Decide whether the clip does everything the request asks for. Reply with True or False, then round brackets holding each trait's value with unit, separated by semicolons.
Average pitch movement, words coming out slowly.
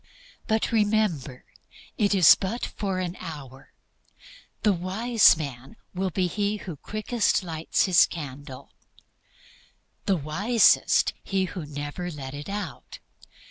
False (5.8 semitones; 120 wpm)